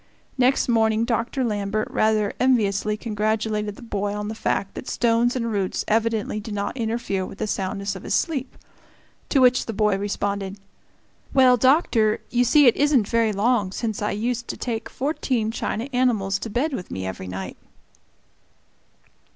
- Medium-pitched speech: No, high, 220 Hz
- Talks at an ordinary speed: Yes, average, 165 wpm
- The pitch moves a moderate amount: Yes, average, 3.2 semitones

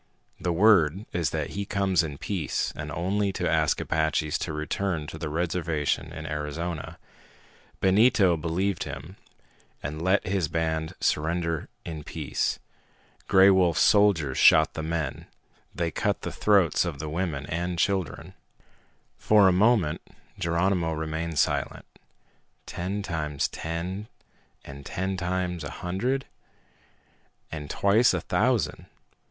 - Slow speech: Yes, slow, 130 wpm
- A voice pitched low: Yes, very low, 85 Hz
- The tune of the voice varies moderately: Yes, average, 3.5 semitones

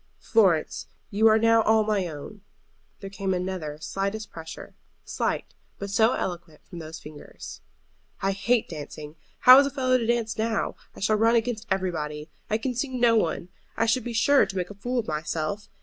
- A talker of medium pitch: No, high, 205 Hz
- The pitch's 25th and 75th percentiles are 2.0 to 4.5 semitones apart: No, average, 5.0 semitones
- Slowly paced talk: No, average, 185 wpm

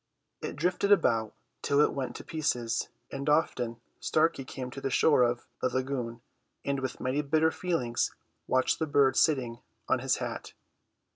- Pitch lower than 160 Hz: Yes, low, 135 Hz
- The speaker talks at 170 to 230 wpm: No, average, 160 wpm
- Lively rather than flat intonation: No, average, 4.0 semitones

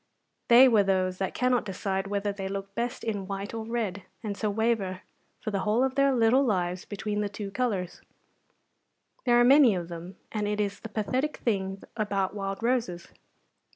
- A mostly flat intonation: No, average, 3.2 semitones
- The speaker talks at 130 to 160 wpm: No, average, 185 wpm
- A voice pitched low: No, high, 205 Hz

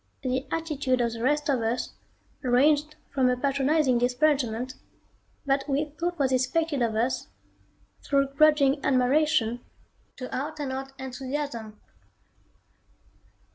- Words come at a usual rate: No, slow, 120 wpm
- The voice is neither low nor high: No, very high, 270 Hz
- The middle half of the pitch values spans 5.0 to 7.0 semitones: No, average, 2.9 semitones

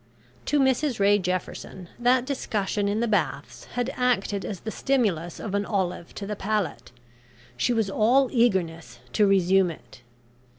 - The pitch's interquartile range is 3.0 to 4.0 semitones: No, average, 4.5 semitones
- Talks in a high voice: Yes, high, 205 Hz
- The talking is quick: No, average, 155 wpm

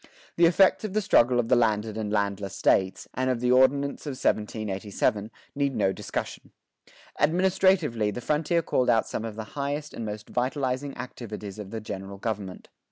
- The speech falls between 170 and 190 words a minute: Yes, average, 175 wpm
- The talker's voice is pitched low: Yes, low, 120 Hz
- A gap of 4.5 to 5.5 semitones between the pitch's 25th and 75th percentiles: Yes, average, 5.1 semitones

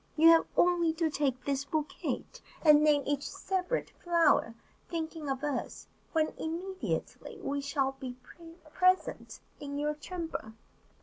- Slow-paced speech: Yes, slow, 130 wpm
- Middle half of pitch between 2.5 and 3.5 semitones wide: Yes, average, 3.2 semitones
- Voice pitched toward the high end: Yes, very high, 310 Hz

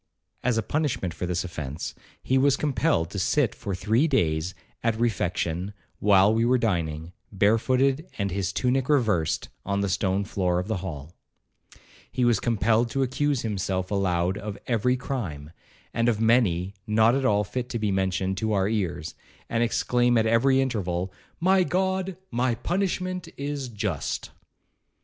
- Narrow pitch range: No, average, 5.3 semitones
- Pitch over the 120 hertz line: No, low, 110 Hz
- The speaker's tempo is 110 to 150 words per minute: No, average, 160 wpm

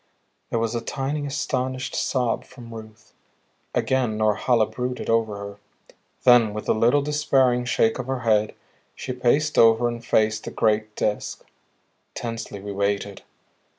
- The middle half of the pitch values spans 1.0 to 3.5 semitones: Yes, average, 2.9 semitones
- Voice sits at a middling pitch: No, low, 115 Hz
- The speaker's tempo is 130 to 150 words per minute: Yes, average, 145 wpm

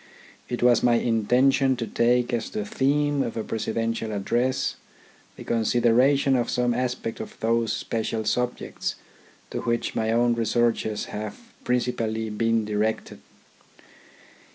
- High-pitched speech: No, low, 120 Hz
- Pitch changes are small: Yes, narrow, 1.8 semitones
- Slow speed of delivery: Yes, slow, 130 wpm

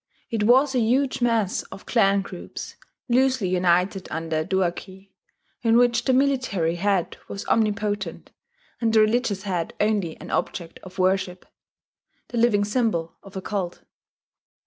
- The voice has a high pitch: Yes, high, 205 Hz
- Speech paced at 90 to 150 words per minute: Yes, average, 145 wpm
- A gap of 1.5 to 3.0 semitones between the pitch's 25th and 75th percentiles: No, average, 4.2 semitones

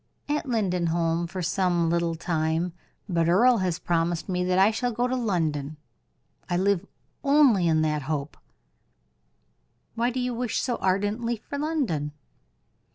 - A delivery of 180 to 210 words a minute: No, average, 145 wpm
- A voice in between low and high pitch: Yes, medium, 180 Hz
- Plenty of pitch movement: Yes, wide, 6.0 semitones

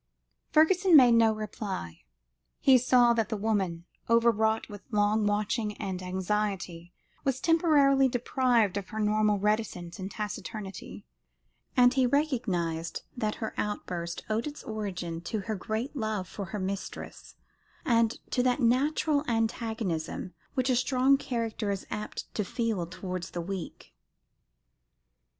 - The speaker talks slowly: Yes, slow, 130 wpm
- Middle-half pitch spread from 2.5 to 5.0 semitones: Yes, average, 4.2 semitones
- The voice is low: No, high, 215 Hz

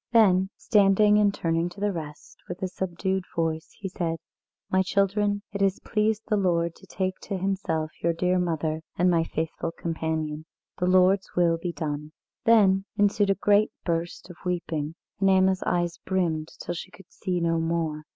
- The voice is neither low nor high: Yes, medium, 180 Hz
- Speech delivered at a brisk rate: No, average, 175 wpm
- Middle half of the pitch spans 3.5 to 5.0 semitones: No, average, 2.9 semitones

